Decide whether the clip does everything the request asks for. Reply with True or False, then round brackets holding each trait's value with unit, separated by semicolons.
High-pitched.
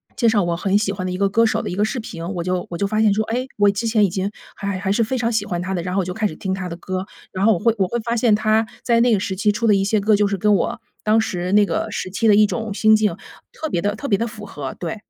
True (205 Hz)